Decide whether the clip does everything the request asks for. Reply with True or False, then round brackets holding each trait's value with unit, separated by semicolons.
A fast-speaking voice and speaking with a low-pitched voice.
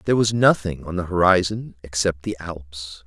False (175 wpm; 90 Hz)